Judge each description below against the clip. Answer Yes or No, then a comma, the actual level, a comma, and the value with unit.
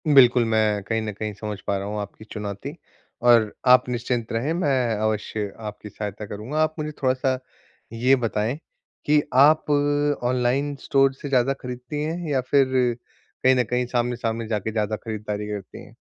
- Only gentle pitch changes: No, average, 3.5 semitones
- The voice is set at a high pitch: No, low, 120 Hz